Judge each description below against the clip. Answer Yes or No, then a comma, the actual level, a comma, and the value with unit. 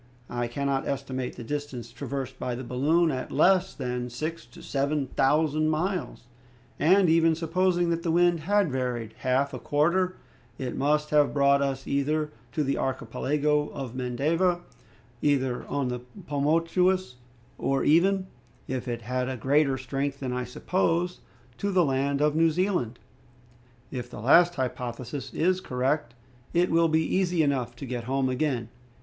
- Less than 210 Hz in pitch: Yes, medium, 140 Hz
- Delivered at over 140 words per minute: Yes, average, 155 wpm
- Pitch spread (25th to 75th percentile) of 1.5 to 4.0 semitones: No, average, 4.4 semitones